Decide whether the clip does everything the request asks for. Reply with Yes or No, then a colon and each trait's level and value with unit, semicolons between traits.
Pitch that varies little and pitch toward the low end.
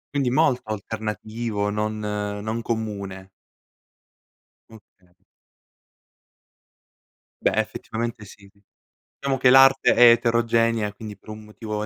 Yes: narrow, 2.1 semitones; low, 110 Hz